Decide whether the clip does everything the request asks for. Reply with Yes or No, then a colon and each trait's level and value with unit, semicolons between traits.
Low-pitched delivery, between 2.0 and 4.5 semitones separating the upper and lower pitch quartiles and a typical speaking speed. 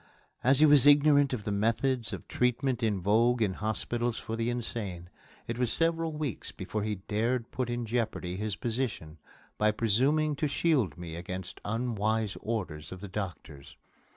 Yes: low, 115 Hz; average, 3.9 semitones; average, 165 wpm